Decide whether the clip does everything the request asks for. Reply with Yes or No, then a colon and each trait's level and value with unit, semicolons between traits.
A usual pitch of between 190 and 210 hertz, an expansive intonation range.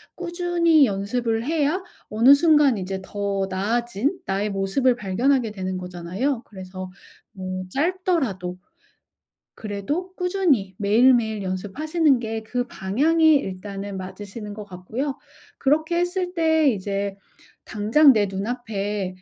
No: high, 225 Hz; wide, 7.2 semitones